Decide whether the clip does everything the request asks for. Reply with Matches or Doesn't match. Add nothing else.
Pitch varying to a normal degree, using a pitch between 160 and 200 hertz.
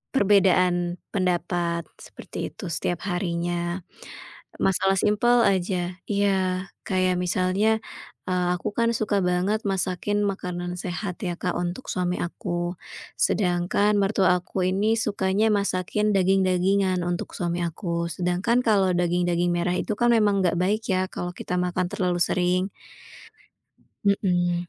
Doesn't match